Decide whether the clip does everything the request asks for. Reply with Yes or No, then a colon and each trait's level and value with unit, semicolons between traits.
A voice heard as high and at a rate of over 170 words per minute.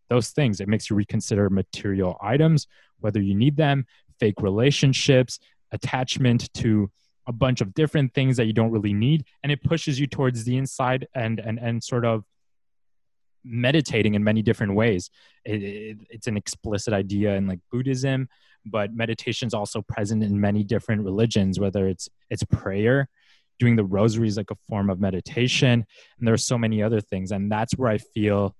No: low, 115 Hz; average, 180 wpm